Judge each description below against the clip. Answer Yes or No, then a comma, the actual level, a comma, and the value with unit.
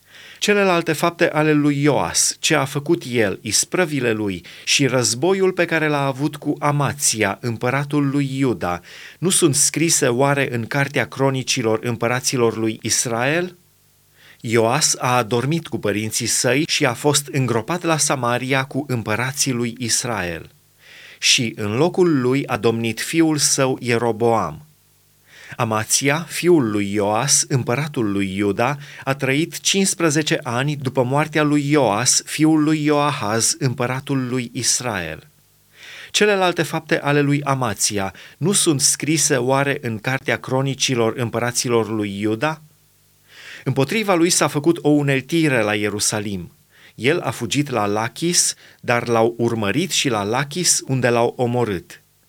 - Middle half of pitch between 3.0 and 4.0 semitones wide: No, average, 4.4 semitones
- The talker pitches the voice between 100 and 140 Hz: Yes, low, 135 Hz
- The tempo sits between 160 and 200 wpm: No, average, 130 wpm